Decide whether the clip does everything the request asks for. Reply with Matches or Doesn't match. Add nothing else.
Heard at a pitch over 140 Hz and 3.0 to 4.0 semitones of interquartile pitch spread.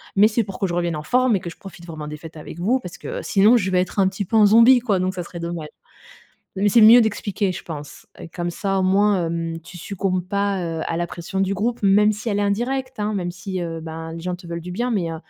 Matches